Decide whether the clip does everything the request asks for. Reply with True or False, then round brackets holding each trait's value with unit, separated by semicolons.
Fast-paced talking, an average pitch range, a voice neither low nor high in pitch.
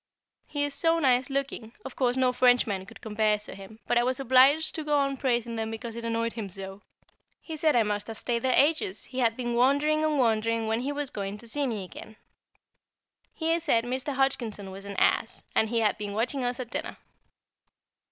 False (210 wpm; 3.7 semitones; 240 Hz)